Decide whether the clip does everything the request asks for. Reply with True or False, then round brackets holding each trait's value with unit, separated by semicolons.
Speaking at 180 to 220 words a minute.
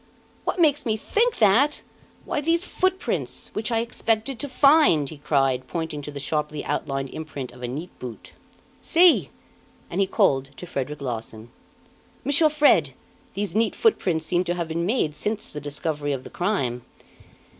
False (165 wpm)